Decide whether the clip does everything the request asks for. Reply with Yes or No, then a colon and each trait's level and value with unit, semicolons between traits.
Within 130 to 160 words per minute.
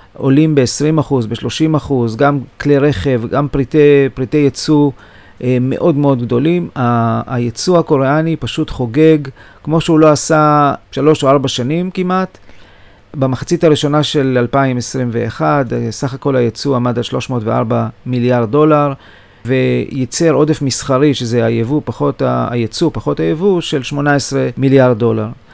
No: average, 115 wpm